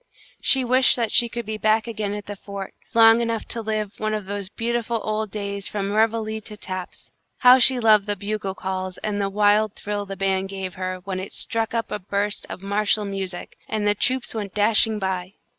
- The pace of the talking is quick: Yes, fast, 210 wpm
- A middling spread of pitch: No, narrow, 2.1 semitones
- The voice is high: Yes, high, 210 Hz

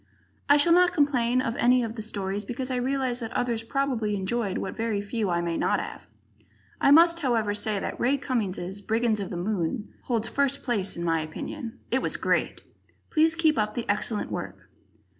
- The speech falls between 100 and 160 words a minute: No, average, 195 wpm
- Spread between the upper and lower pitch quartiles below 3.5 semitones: No, average, 4.3 semitones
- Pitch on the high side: Yes, high, 230 Hz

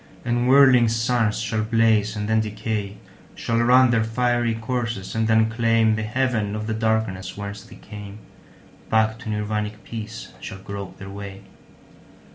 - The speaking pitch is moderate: No, low, 110 Hz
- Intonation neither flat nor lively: No, narrow, 1.7 semitones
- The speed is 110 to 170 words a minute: Yes, average, 140 wpm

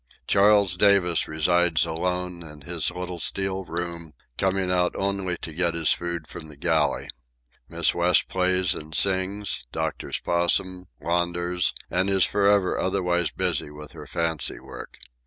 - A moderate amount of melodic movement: No, narrow, 2.0 semitones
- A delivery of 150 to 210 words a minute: No, average, 140 wpm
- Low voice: Yes, very low, 90 Hz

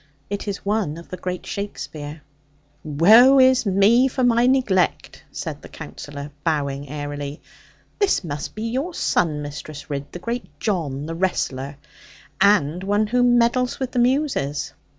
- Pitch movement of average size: No, wide, 8.5 semitones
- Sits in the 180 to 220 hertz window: Yes, high, 190 Hz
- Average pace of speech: Yes, average, 150 wpm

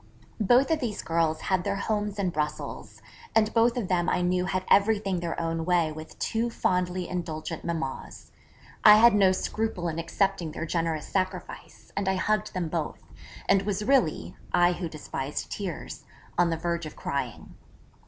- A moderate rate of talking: Yes, average, 170 wpm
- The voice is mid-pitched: Yes, medium, 180 Hz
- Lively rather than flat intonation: No, average, 3.7 semitones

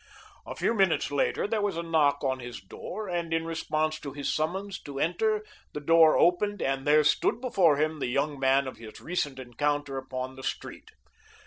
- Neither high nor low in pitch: Yes, medium, 155 Hz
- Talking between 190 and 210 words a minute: Yes, average, 195 wpm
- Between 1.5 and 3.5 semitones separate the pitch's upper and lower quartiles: No, average, 4.2 semitones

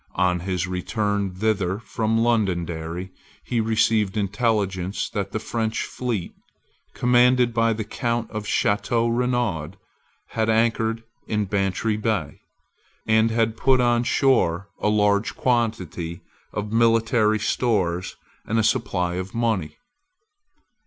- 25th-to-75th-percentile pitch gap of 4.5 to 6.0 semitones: No, average, 3.3 semitones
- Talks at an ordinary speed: No, slow, 120 wpm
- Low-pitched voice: Yes, low, 110 Hz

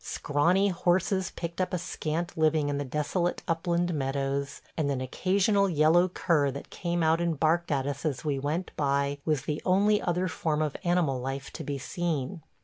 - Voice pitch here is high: No, medium, 160 Hz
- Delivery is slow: No, average, 185 wpm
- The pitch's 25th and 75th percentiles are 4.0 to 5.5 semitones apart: No, average, 3.6 semitones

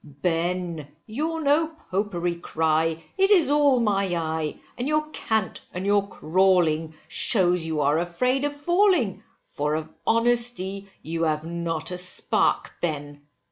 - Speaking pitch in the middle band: Yes, medium, 180 Hz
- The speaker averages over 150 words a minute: No, average, 140 wpm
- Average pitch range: No, wide, 7.0 semitones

